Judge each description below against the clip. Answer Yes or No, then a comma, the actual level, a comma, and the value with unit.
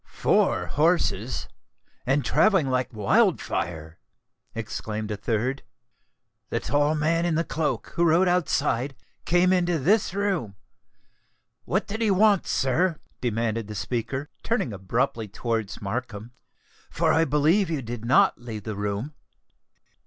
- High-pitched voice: No, low, 130 Hz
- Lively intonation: Yes, wide, 7.4 semitones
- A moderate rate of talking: No, slow, 130 wpm